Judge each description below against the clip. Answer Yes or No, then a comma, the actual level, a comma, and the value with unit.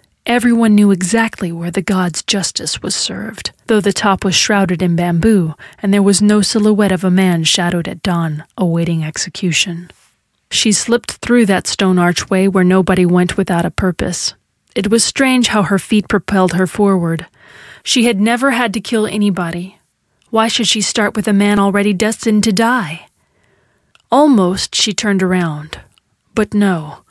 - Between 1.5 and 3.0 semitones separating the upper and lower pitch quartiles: No, average, 3.4 semitones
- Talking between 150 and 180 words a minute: Yes, average, 165 wpm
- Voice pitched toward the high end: Yes, high, 195 Hz